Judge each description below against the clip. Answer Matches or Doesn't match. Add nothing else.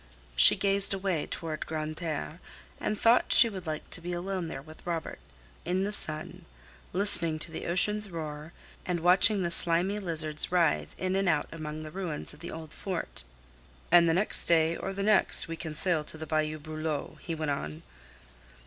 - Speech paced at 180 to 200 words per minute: Matches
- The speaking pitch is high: Doesn't match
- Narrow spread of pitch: Doesn't match